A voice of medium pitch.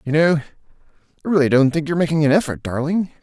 Yes: medium, 155 Hz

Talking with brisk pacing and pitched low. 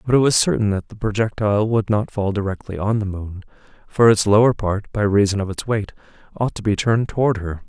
Yes: fast, 225 wpm; low, 105 Hz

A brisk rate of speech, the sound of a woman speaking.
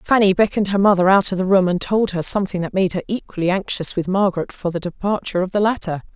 Yes: fast, 245 wpm; female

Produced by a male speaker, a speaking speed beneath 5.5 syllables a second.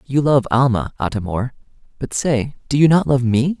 Yes: male; 4.9 syllables/s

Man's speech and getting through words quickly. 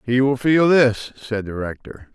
No: male; average, 195 wpm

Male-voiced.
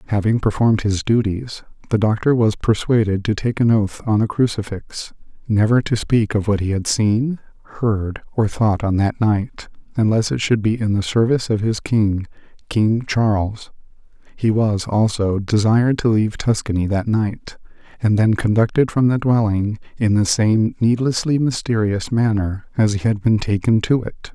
Yes: male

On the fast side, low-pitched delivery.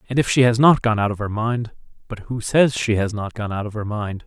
Yes: fast, 295 wpm; low, 110 Hz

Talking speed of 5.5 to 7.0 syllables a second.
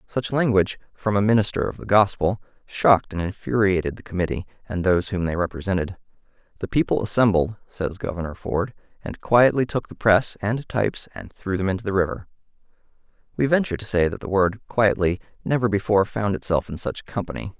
Yes: 5.9 syllables/s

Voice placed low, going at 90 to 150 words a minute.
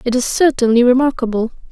No: very high, 250 Hz; average, 140 wpm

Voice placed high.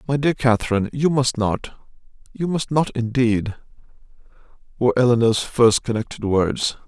No: low, 120 Hz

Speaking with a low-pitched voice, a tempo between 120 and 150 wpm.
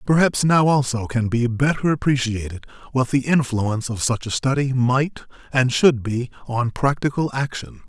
No: low, 130 Hz; average, 160 wpm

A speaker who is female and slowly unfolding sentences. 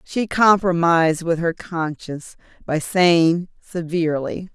Yes: female; slow, 105 wpm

